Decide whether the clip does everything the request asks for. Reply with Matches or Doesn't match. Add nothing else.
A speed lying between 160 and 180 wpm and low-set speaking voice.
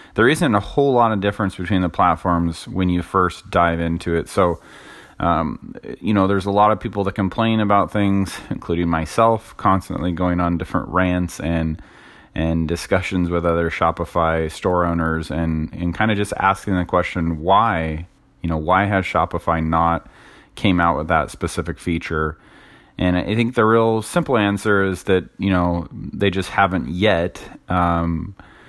Matches